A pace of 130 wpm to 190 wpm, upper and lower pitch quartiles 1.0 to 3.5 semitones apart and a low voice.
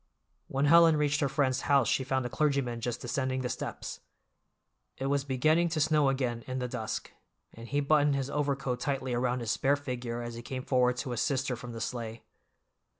No: average, 200 wpm; narrow, 2.6 semitones; low, 130 Hz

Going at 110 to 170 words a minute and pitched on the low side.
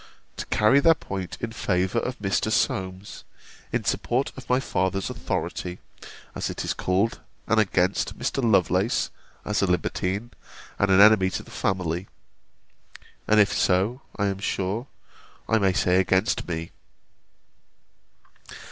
Yes: average, 140 wpm; low, 100 Hz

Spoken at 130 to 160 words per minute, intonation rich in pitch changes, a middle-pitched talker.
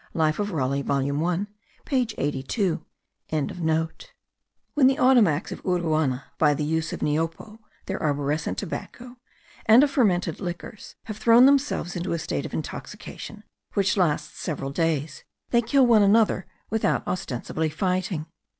Yes: average, 140 wpm; wide, 6.1 semitones; medium, 175 Hz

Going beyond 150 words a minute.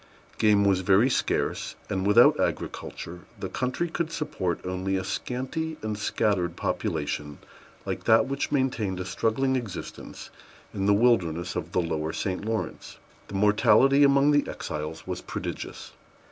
No: average, 145 wpm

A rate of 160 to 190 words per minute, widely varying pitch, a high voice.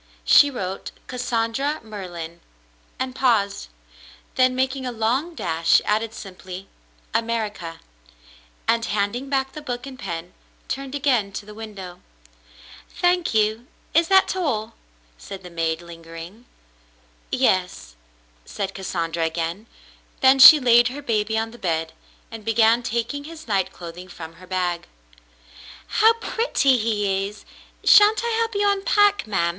No: average, 140 wpm; wide, 6.4 semitones; high, 220 Hz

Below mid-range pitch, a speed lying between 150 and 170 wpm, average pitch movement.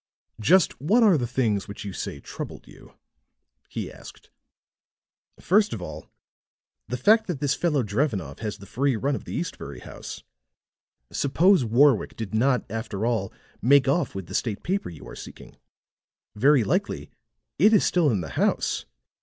No: low, 130 Hz; average, 160 wpm; wide, 6.9 semitones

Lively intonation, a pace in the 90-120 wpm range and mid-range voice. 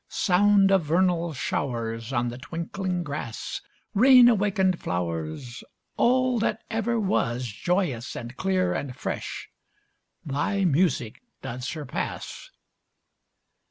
Yes: wide, 8.3 semitones; slow, 105 wpm; medium, 170 Hz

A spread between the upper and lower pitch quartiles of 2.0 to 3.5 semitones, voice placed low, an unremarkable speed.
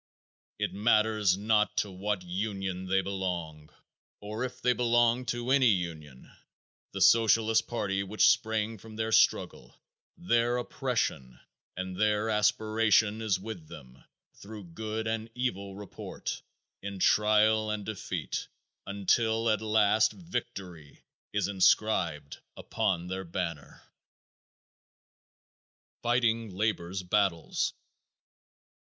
No: average, 3.0 semitones; low, 105 Hz; slow, 110 wpm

